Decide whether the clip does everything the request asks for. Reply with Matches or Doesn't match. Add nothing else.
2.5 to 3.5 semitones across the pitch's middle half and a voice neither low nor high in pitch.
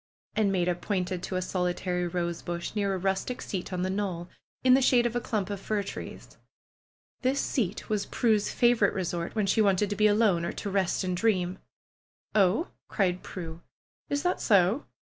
Doesn't match